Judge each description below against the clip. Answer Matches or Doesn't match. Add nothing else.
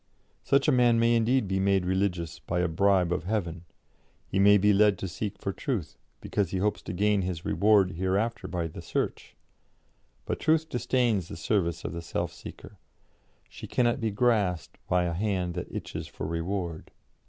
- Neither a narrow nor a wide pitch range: Matches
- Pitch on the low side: Matches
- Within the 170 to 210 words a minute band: Matches